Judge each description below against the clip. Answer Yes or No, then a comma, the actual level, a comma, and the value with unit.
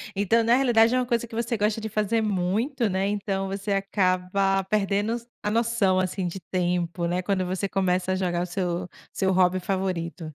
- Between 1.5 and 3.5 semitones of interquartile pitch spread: Yes, average, 3.0 semitones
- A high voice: Yes, high, 195 Hz